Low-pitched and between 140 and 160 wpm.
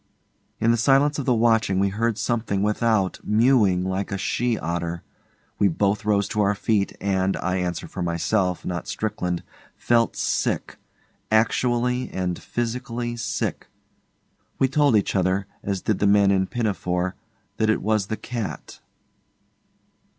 Yes: low, 105 Hz; average, 145 wpm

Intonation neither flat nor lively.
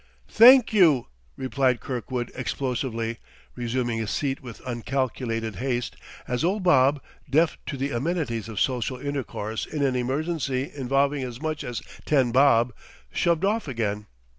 Yes: average, 3.2 semitones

